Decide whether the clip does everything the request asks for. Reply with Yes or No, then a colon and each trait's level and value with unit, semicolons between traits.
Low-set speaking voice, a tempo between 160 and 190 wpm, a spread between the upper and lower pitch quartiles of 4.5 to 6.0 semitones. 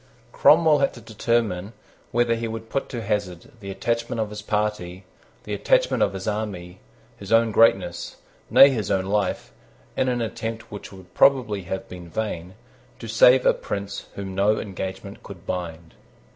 No: low, 105 Hz; average, 165 wpm; average, 3.4 semitones